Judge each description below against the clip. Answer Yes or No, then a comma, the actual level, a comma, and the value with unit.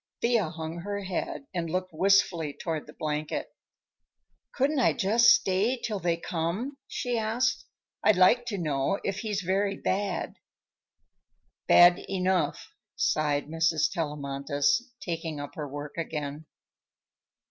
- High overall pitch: No, medium, 175 Hz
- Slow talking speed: Yes, slow, 125 wpm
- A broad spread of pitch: No, average, 4.7 semitones